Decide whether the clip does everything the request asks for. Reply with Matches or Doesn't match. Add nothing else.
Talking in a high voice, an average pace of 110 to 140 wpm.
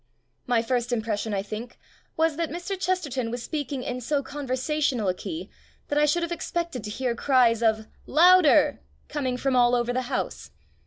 Doesn't match